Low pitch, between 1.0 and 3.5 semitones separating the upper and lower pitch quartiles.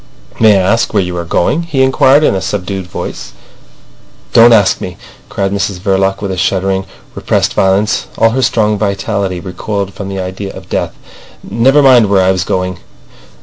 Yes: low, 100 Hz; average, 2.9 semitones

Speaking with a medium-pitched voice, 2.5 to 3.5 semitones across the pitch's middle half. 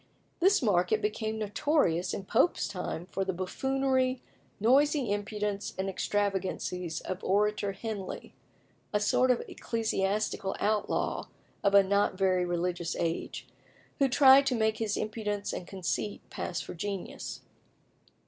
No: high, 205 Hz; average, 3.0 semitones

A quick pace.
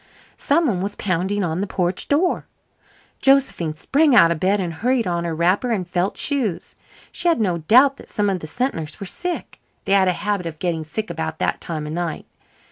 Yes: fast, 210 wpm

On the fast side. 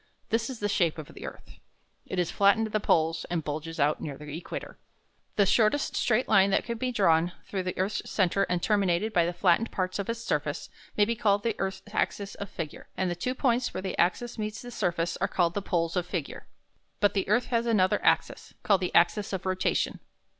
Yes: fast, 220 wpm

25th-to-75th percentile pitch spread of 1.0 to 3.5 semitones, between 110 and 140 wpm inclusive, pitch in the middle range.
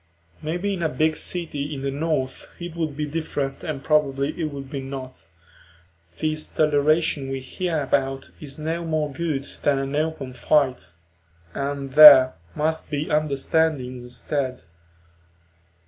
Yes: narrow, 2.6 semitones; slow, 135 wpm; medium, 145 Hz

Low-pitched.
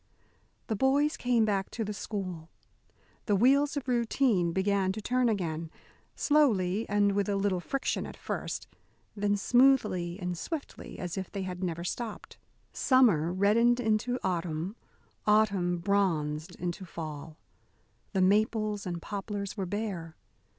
No: high, 200 Hz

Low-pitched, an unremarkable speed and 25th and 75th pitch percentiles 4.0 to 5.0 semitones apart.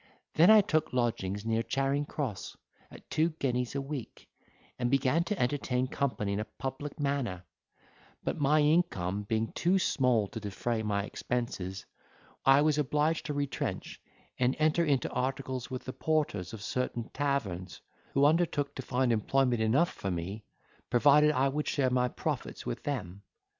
Yes: low, 130 Hz; average, 160 wpm; average, 4.6 semitones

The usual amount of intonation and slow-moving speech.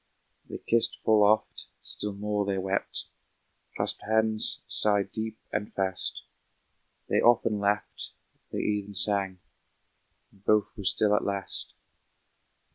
No: narrow, 1.4 semitones; slow, 120 wpm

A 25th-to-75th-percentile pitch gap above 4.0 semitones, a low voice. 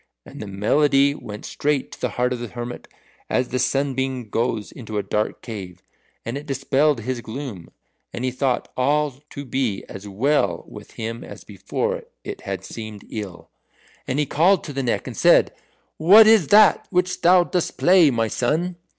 Yes: average, 4.8 semitones; low, 130 Hz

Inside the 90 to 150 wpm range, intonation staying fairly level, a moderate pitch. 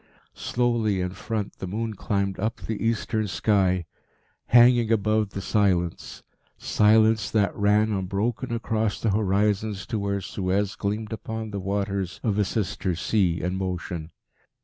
No: average, 140 wpm; narrow, 2.3 semitones; low, 105 Hz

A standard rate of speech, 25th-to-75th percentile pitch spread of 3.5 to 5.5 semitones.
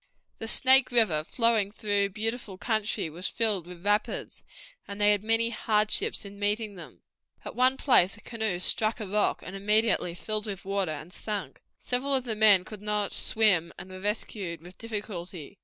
No: average, 175 wpm; average, 3.0 semitones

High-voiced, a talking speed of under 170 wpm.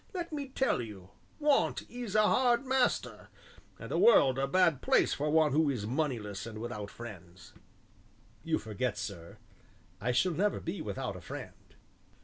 No: low, 135 Hz; average, 160 wpm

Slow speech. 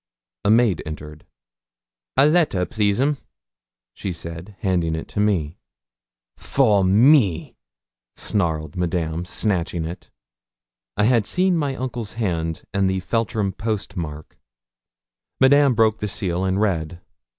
Yes: slow, 125 wpm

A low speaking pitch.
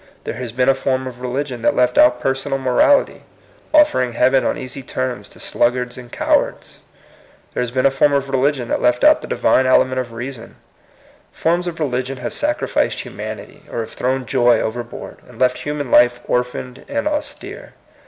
Yes: low, 130 Hz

